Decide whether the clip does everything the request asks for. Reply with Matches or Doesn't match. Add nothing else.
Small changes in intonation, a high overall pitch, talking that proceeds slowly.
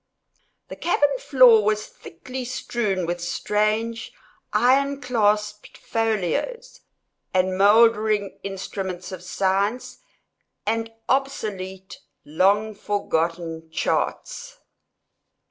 Doesn't match